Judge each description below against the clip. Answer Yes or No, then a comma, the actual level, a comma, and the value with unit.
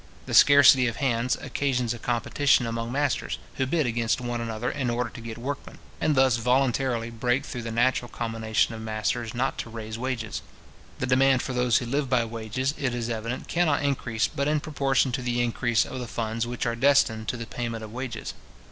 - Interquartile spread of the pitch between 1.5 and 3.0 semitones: Yes, narrow, 2.4 semitones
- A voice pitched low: Yes, low, 120 Hz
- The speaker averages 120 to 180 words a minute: No, average, 200 wpm